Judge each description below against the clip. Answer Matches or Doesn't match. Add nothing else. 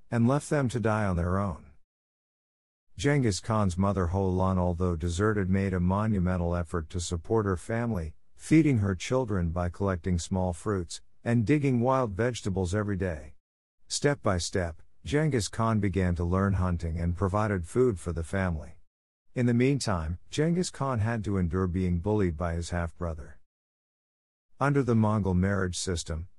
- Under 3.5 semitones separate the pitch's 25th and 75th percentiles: Doesn't match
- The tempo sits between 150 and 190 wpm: Matches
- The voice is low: Matches